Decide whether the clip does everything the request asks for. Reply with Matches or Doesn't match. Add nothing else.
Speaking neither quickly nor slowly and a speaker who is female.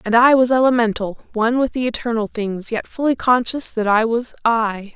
Matches